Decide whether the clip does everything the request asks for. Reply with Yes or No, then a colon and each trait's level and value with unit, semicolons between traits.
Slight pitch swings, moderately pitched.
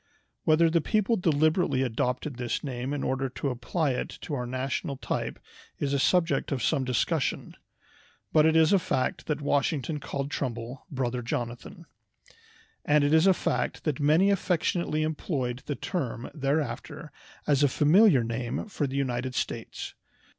No: average, 3.7 semitones; medium, 145 Hz